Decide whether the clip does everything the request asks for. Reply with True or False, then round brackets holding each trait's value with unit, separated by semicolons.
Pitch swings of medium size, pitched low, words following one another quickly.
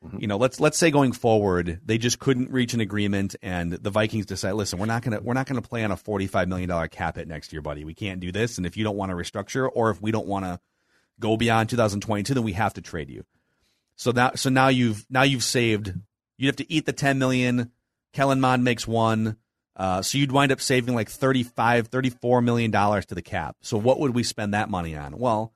True (4.2 semitones; 110 Hz; 245 wpm)